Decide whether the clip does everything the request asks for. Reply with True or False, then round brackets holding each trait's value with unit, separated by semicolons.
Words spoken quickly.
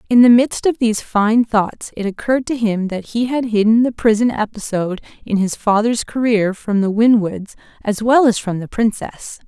False (195 wpm)